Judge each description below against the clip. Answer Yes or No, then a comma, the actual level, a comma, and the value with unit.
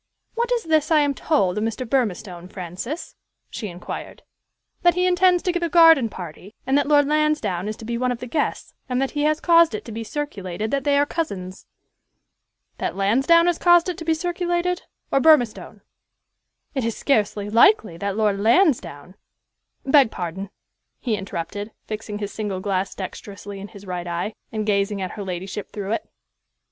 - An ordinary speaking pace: Yes, average, 180 wpm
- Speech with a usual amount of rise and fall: No, wide, 7.6 semitones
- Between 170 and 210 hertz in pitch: No, high, 225 Hz